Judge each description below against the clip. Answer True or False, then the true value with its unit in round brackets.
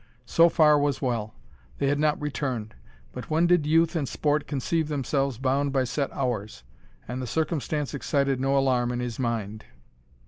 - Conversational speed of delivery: True (170 wpm)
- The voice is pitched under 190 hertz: True (140 Hz)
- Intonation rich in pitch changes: False (3.4 semitones)